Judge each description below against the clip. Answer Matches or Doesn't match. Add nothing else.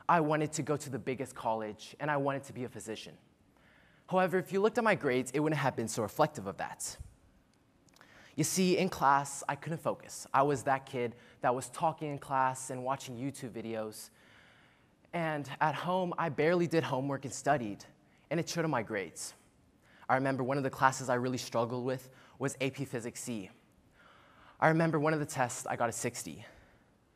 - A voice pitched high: Doesn't match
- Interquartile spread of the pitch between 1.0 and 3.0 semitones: Doesn't match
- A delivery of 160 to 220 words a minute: Matches